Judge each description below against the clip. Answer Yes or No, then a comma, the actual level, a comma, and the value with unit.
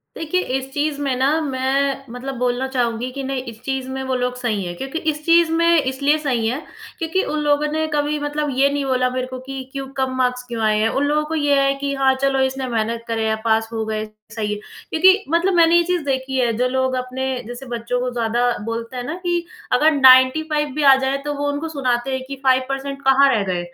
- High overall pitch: Yes, very high, 265 Hz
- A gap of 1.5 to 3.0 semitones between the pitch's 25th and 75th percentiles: Yes, average, 2.7 semitones